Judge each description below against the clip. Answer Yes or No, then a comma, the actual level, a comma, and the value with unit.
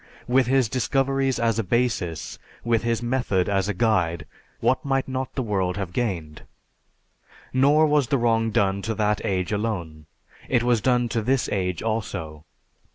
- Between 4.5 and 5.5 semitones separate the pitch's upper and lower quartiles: Yes, average, 4.9 semitones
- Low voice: Yes, low, 115 Hz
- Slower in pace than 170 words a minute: Yes, average, 160 wpm